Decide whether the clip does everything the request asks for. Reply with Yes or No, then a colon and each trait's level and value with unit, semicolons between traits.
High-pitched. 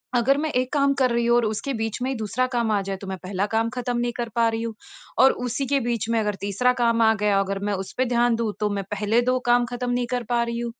Yes: high, 235 Hz